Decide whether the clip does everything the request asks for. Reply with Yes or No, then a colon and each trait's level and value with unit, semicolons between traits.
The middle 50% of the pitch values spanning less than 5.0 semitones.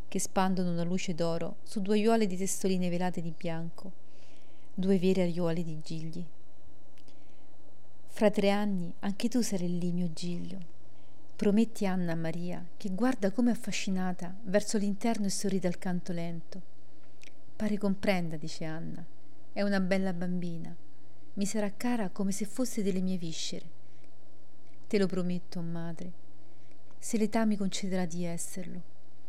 Yes: average, 2.7 semitones